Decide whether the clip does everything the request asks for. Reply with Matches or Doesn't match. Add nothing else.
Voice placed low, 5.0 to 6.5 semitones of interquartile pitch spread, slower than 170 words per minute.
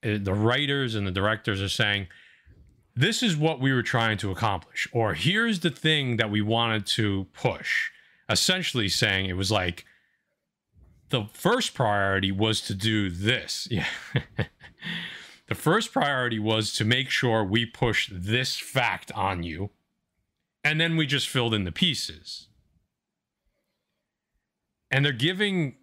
Matches